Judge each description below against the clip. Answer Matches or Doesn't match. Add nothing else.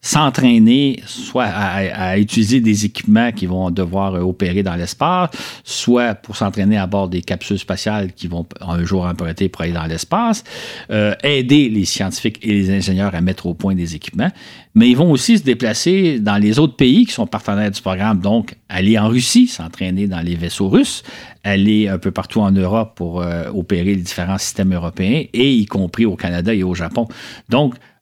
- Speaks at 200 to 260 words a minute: Doesn't match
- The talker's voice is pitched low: Matches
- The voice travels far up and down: Doesn't match